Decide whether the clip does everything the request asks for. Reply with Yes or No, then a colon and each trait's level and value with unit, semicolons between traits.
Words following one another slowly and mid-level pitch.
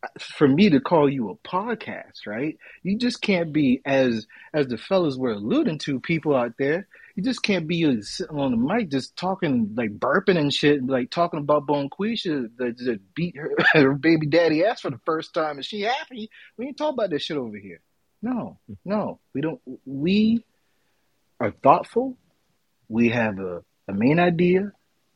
No: average, 185 wpm; medium, 165 Hz